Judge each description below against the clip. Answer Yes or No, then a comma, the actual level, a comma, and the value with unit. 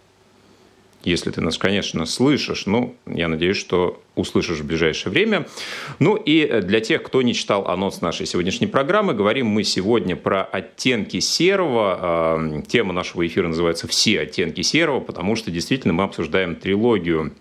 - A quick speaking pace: No, average, 150 wpm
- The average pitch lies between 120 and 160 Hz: No, very low, 85 Hz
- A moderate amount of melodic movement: No, narrow, 2.0 semitones